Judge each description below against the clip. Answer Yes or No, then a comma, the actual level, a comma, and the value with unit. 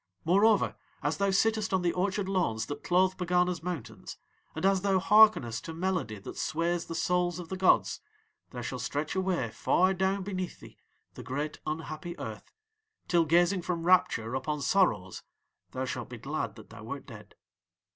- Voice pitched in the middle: Yes, medium, 175 Hz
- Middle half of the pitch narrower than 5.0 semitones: Yes, average, 3.6 semitones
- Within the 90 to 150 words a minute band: No, average, 170 wpm